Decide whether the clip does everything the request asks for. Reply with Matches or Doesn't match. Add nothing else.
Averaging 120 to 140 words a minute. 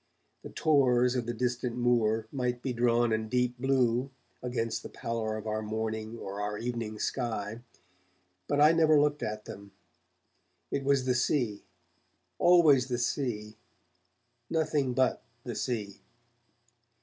Matches